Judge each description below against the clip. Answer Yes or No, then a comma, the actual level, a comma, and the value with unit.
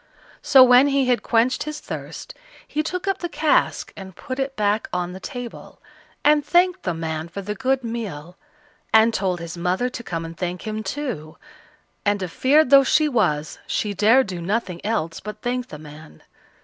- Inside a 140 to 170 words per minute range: No, average, 190 wpm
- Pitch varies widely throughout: Yes, wide, 6.8 semitones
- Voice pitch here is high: Yes, high, 215 Hz